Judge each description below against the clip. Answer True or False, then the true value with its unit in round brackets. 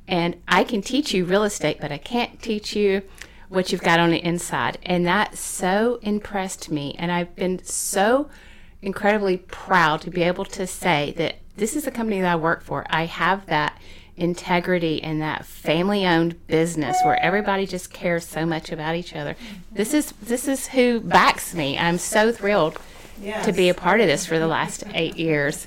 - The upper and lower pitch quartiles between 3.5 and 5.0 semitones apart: True (4.0 semitones)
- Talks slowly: False (190 wpm)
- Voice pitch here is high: False (180 Hz)